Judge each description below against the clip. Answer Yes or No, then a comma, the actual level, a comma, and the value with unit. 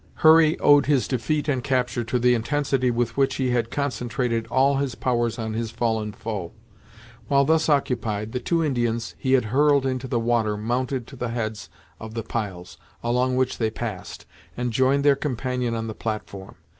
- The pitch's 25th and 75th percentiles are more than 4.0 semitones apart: No, average, 3.0 semitones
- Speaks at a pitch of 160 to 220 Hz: No, low, 125 Hz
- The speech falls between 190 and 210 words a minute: No, average, 180 wpm